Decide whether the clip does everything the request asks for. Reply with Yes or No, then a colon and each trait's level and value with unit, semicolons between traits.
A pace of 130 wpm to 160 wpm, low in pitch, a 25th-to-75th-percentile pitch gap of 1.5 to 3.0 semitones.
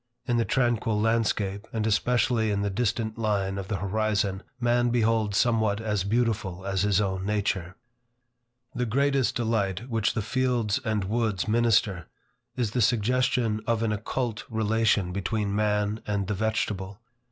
Yes: average, 150 wpm; low, 110 Hz; narrow, 2.5 semitones